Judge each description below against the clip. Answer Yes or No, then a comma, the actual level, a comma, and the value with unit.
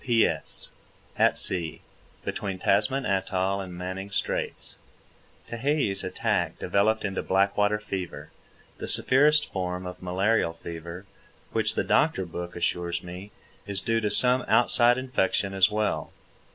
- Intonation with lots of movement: No, average, 3.4 semitones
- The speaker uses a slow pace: Yes, slow, 125 wpm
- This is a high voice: No, very low, 95 Hz